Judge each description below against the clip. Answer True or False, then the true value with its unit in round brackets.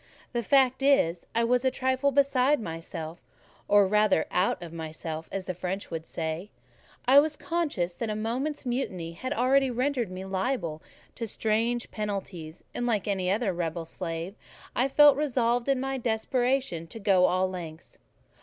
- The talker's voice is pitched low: False (215 Hz)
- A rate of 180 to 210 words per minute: False (165 wpm)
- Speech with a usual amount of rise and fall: False (6.6 semitones)